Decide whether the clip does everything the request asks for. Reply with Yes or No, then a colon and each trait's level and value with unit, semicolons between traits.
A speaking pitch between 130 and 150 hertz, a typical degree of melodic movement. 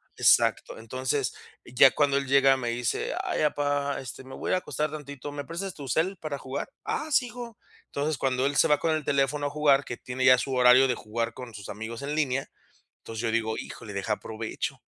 Yes: low, 135 Hz; average, 3.0 semitones